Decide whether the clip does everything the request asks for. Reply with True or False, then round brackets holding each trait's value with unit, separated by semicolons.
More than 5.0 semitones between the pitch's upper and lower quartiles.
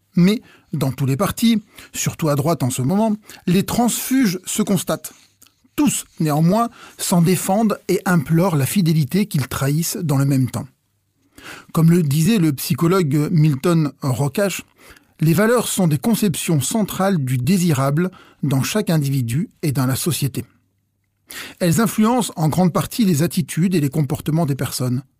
True (5.5 semitones)